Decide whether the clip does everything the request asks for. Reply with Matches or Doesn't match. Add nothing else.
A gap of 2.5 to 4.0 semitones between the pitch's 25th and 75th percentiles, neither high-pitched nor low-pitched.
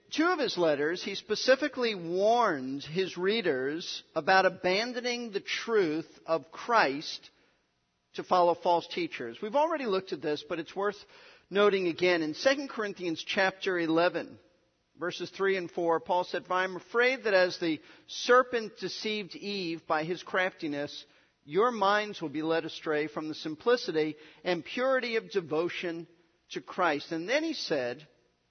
Doesn't match